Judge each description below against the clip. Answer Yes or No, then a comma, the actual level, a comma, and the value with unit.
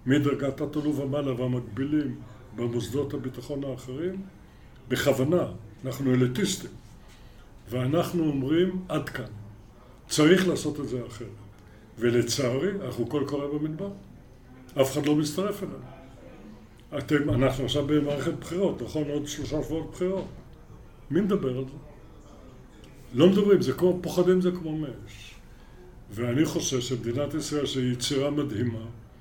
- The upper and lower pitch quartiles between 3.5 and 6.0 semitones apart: Yes, average, 3.9 semitones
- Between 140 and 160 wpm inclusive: No, average, 120 wpm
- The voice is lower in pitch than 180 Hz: Yes, medium, 140 Hz